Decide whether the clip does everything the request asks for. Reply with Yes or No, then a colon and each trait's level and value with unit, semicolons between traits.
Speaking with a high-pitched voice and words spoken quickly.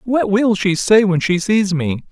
Yes: high, 195 Hz; fast, 225 wpm